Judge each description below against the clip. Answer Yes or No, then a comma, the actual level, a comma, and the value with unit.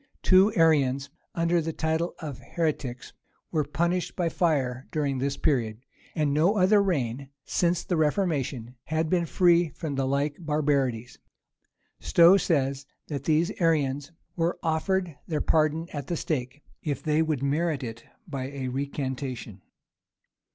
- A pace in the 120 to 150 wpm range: Yes, average, 140 wpm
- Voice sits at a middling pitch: Yes, medium, 150 Hz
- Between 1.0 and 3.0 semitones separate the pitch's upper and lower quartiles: No, average, 3.7 semitones